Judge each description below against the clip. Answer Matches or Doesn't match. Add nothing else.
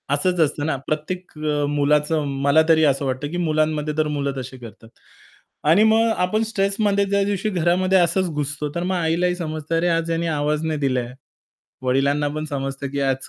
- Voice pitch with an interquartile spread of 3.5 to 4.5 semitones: Matches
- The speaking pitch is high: Doesn't match